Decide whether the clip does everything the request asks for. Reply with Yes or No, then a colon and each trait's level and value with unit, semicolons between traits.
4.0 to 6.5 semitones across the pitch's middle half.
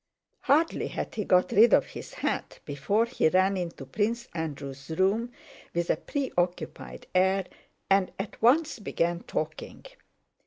Yes: average, 5.2 semitones